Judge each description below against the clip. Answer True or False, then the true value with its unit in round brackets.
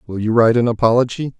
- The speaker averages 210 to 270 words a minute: True (215 wpm)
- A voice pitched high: False (115 Hz)